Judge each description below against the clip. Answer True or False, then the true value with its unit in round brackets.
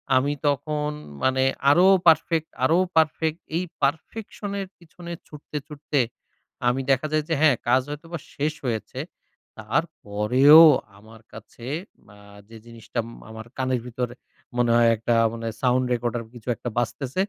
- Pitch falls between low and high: False (130 Hz)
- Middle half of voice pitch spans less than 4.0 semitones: False (4.6 semitones)